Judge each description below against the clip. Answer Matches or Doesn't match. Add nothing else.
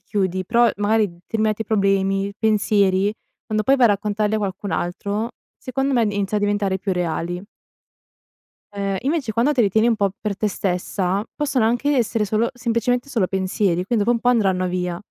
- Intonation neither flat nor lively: Matches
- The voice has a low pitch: Doesn't match